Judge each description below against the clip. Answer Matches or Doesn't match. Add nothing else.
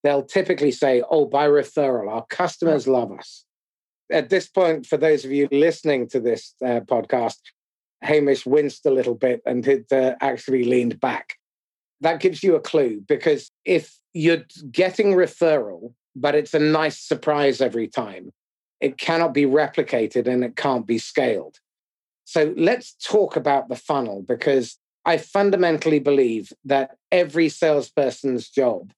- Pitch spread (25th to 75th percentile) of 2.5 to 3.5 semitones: Doesn't match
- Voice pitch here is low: Doesn't match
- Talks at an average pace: Matches